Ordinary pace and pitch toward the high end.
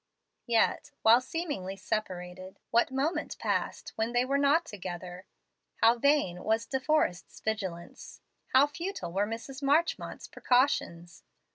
No: slow, 125 wpm; high, 230 Hz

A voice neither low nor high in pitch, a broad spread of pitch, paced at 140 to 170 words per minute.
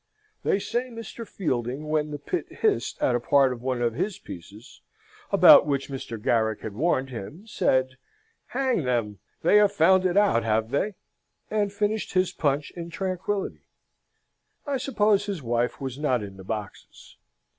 Yes: medium, 150 Hz; wide, 9.0 semitones; average, 165 wpm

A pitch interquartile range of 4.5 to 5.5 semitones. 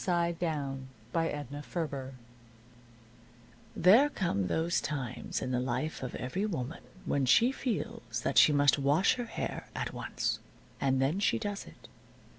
Yes: average, 5.2 semitones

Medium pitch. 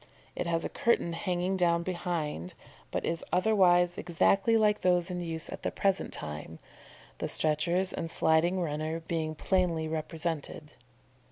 Yes: medium, 170 Hz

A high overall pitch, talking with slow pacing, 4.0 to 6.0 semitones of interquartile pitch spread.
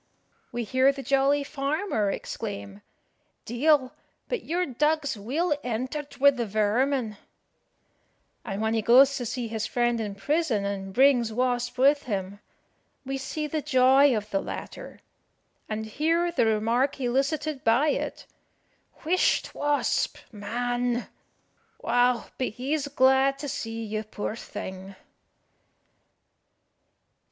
Yes: very high, 250 Hz; slow, 125 wpm; average, 4.3 semitones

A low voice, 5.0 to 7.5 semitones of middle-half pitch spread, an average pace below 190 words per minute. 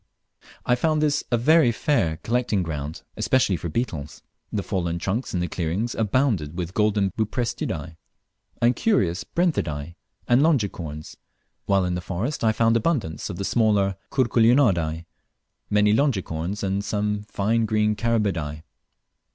Yes: low, 105 Hz; average, 5.3 semitones; slow, 135 wpm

